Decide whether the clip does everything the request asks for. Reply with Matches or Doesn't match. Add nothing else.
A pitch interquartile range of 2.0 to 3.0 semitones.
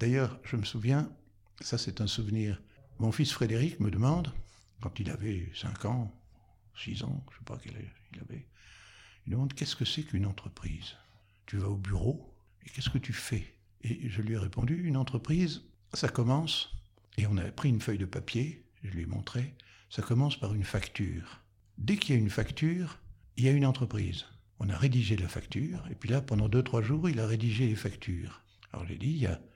Doesn't match